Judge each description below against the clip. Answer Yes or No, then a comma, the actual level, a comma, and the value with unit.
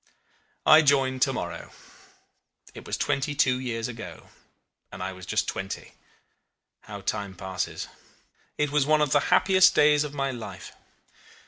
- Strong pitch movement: No, average, 4.5 semitones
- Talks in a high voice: No, low, 135 Hz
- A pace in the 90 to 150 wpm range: Yes, average, 145 wpm